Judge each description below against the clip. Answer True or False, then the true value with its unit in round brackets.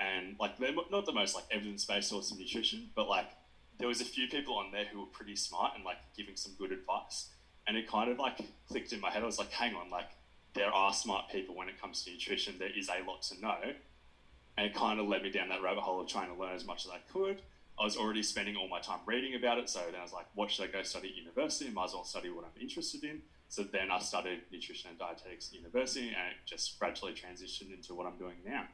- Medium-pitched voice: False (105 Hz)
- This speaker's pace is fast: True (270 wpm)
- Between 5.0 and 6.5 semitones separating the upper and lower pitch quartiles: True (5.3 semitones)